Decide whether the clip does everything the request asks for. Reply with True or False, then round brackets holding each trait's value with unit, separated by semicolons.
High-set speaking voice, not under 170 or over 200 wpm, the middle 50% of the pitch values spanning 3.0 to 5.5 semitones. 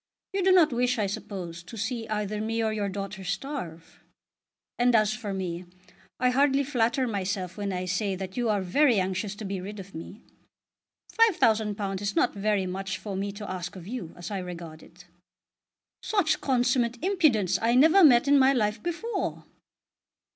True (210 Hz; 175 wpm; 4.6 semitones)